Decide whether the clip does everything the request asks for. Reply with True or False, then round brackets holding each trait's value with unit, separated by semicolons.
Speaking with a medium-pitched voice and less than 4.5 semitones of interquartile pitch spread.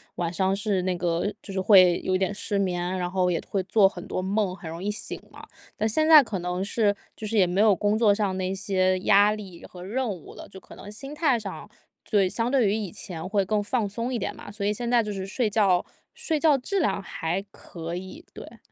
False (200 Hz; 2.8 semitones)